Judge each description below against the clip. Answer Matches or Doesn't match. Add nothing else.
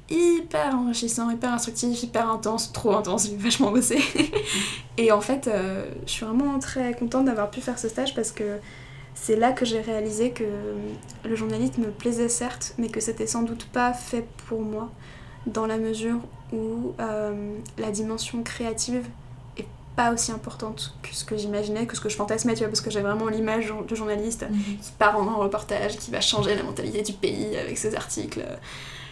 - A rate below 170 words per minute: Doesn't match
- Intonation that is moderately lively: Doesn't match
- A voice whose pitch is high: Matches